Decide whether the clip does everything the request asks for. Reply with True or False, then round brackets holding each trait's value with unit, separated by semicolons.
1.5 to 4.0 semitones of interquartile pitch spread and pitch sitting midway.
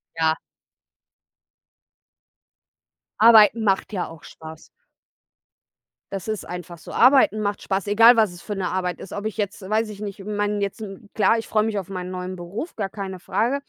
False (2.8 semitones; 200 Hz)